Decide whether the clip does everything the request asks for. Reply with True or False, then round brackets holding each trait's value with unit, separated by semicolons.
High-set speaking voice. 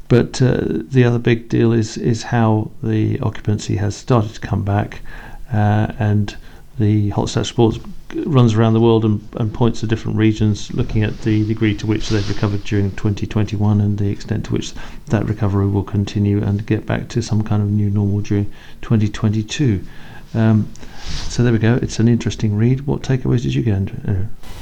False (110 Hz)